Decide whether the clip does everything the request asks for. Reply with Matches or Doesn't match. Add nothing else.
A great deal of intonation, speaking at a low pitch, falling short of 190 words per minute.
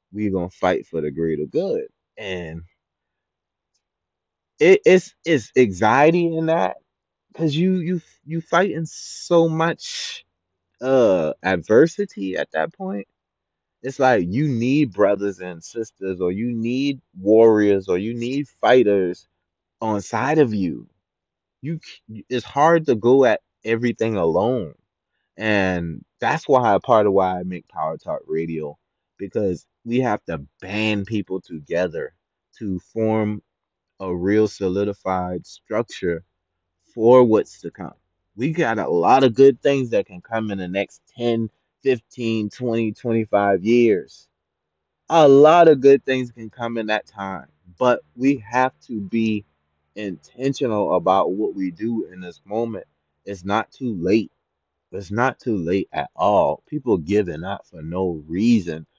Matches